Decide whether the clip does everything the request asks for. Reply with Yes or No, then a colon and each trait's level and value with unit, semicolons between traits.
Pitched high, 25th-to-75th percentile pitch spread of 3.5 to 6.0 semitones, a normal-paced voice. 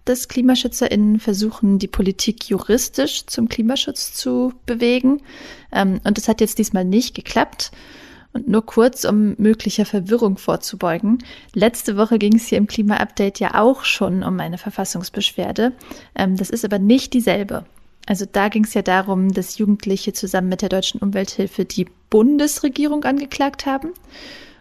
Yes: high, 215 Hz; average, 3.9 semitones; average, 145 wpm